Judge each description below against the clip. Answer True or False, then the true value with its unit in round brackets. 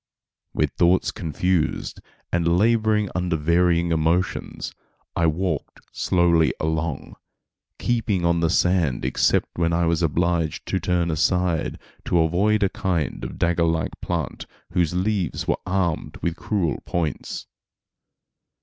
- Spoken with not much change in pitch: True (1.9 semitones)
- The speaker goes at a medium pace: False (125 wpm)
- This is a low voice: True (85 Hz)